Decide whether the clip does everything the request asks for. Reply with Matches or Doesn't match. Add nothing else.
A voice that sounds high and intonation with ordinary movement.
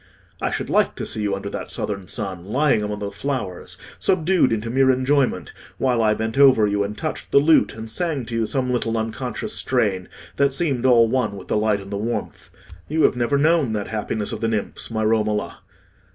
Doesn't match